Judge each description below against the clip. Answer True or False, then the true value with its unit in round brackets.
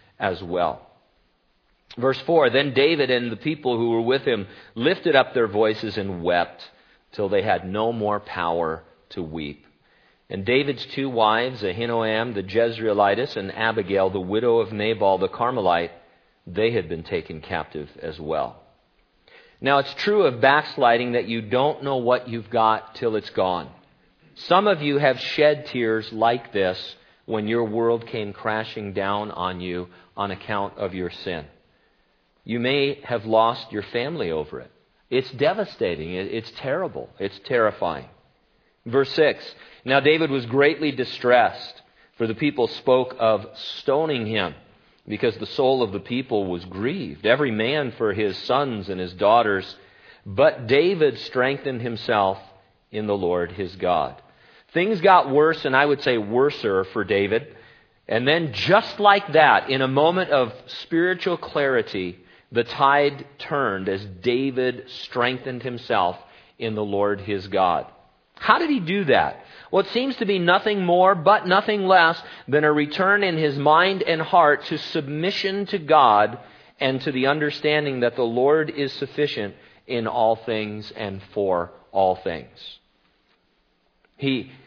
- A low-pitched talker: True (120 Hz)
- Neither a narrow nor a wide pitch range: False (6.2 semitones)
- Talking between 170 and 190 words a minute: False (150 wpm)